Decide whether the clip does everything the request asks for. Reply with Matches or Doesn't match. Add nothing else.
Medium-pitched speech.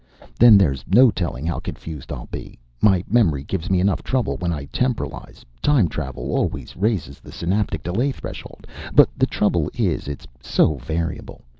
Doesn't match